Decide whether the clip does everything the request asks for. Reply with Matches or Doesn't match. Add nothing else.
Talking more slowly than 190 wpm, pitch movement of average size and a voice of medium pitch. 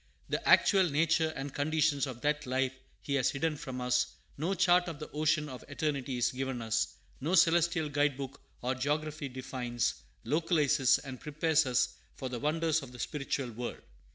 Matches